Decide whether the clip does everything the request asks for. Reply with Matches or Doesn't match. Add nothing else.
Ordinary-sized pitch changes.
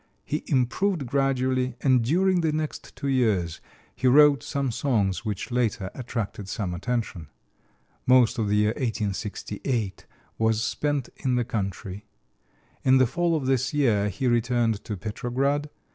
Matches